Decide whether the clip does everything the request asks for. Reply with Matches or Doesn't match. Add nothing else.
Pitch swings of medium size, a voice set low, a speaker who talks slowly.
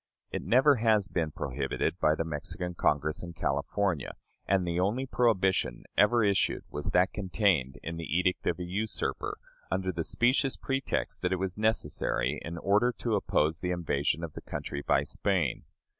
Doesn't match